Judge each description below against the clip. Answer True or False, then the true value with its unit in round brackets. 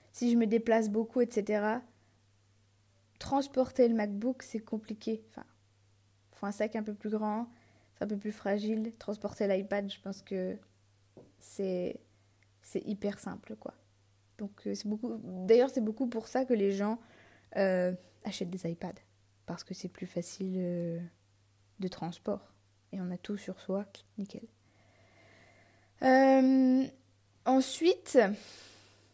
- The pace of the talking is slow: True (140 wpm)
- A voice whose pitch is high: True (195 Hz)